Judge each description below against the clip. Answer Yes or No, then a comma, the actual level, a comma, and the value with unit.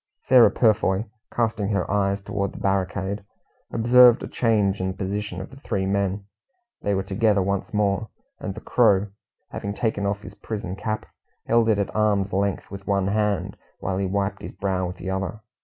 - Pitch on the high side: No, low, 100 Hz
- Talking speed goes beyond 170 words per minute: Yes, average, 185 wpm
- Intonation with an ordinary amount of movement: No, narrow, 1.7 semitones